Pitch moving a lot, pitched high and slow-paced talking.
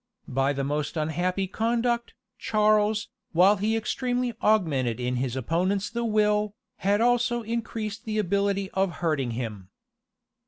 Yes: wide, 6.0 semitones; high, 200 Hz; slow, 130 wpm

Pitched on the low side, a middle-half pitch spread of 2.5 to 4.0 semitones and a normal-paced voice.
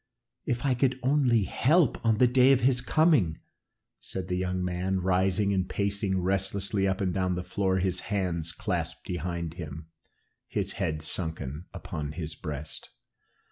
Yes: very low, 95 Hz; average, 3.5 semitones; average, 155 wpm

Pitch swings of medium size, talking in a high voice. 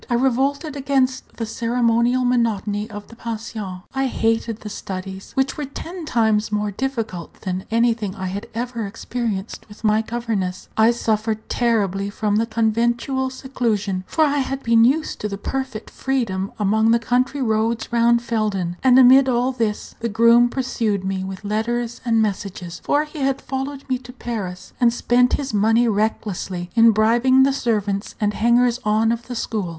Yes: average, 3.0 semitones; high, 230 Hz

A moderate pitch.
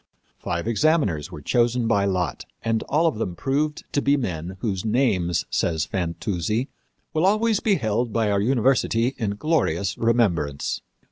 No: low, 110 Hz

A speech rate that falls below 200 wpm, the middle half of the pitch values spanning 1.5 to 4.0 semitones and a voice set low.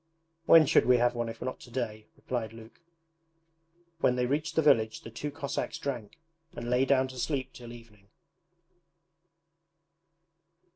Yes: average, 150 wpm; average, 3.3 semitones; low, 125 Hz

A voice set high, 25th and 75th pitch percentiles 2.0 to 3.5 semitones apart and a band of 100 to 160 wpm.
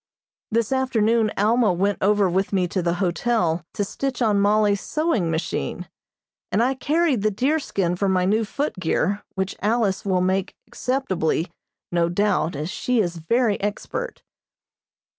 No: high, 205 Hz; average, 4.4 semitones; average, 145 wpm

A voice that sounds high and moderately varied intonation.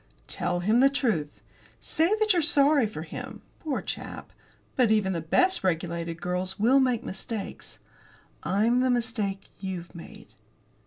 No: high, 215 Hz; wide, 6.5 semitones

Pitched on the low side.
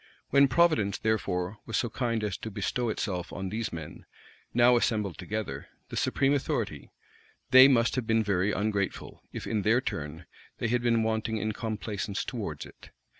Yes: low, 110 Hz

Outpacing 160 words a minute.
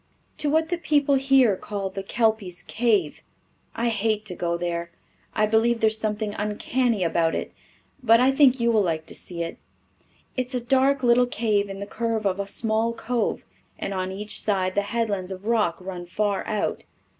Yes: average, 190 wpm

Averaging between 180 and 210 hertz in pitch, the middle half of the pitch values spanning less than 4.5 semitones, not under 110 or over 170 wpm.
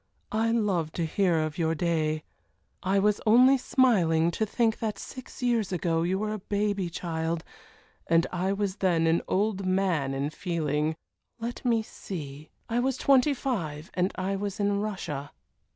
No: high, 190 Hz; average, 4.8 semitones; average, 165 wpm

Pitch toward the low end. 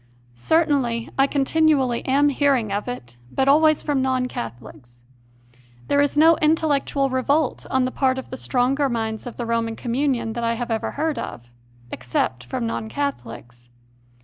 No: very high, 250 Hz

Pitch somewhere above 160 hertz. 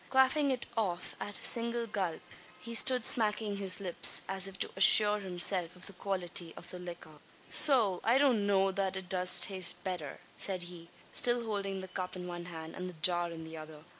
Yes: high, 190 Hz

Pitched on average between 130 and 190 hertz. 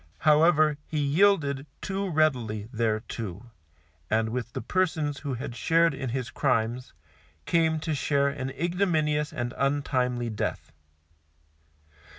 Yes: medium, 140 Hz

